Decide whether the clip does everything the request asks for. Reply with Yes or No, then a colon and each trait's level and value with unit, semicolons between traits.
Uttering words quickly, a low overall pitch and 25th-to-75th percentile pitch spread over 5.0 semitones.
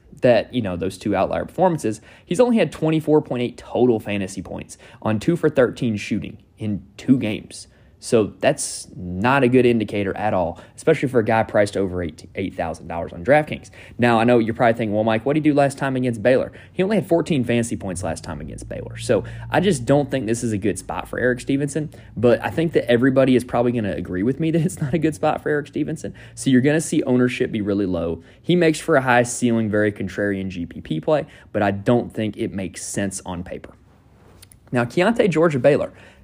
Yes: fast, 215 wpm; low, 115 Hz; wide, 5.5 semitones